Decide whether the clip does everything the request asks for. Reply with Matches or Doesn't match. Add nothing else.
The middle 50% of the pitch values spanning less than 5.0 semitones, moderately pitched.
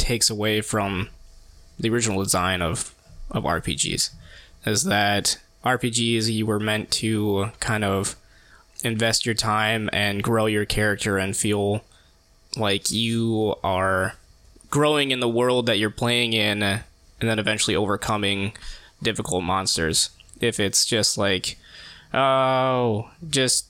Doesn't match